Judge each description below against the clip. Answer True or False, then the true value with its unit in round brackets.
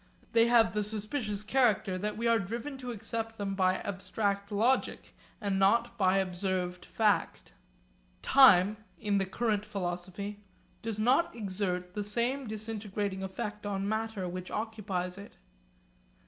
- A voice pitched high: True (210 Hz)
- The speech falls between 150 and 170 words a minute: False (135 wpm)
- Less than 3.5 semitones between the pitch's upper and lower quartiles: True (2.8 semitones)